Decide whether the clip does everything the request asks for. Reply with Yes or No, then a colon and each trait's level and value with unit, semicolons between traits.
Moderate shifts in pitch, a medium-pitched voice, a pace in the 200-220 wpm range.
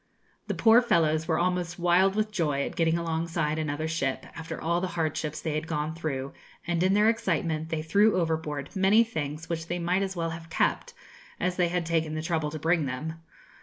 No: narrow, 2.2 semitones; medium, 165 Hz; fast, 205 wpm